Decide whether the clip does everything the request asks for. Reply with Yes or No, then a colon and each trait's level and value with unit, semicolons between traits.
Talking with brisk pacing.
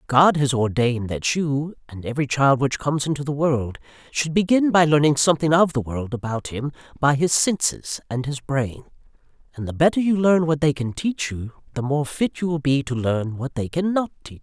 Yes: fast, 215 wpm